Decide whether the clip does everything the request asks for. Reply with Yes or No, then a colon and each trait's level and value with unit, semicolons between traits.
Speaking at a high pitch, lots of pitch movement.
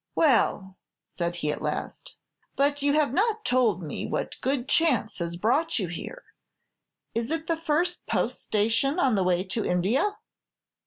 Yes: very high, 250 Hz; wide, 8.7 semitones